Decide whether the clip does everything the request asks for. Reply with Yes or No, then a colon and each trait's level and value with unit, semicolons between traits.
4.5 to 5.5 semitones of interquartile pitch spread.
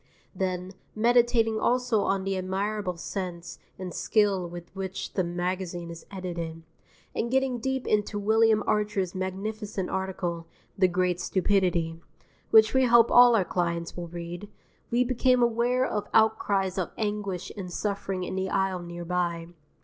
No: average, 3.6 semitones